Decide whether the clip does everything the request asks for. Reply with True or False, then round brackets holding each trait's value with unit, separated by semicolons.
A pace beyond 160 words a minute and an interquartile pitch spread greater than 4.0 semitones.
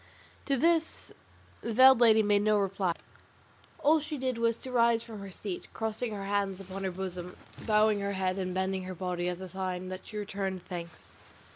False (190 wpm; 3.4 semitones)